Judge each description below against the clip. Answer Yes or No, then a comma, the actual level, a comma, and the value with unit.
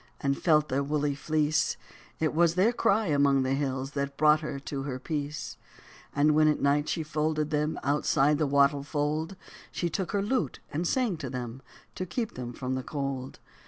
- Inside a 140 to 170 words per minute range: No, average, 195 wpm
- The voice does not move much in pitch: Yes, narrow, 2.2 semitones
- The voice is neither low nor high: Yes, medium, 150 Hz